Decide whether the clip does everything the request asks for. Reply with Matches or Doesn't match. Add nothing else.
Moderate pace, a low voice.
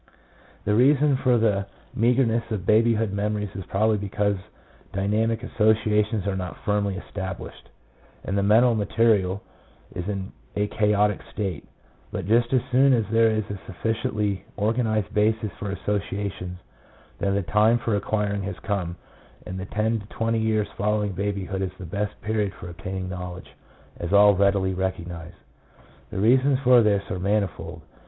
Matches